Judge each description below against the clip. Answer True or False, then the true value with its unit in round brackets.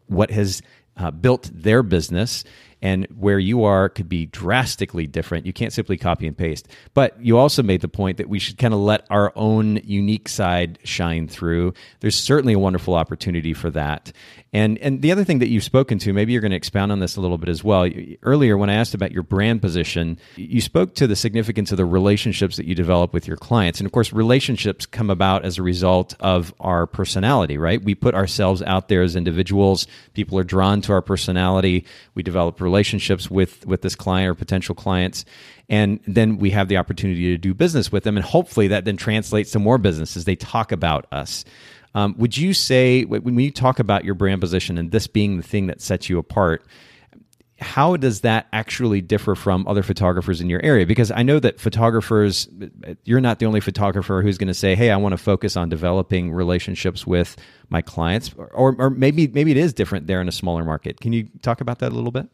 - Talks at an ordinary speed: False (215 wpm)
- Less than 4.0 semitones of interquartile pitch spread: True (3.5 semitones)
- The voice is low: True (100 Hz)